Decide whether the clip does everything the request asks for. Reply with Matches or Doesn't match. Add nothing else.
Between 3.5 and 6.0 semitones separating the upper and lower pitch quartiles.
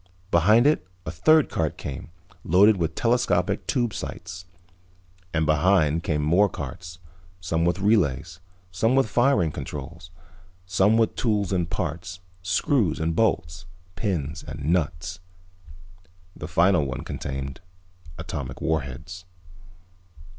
Matches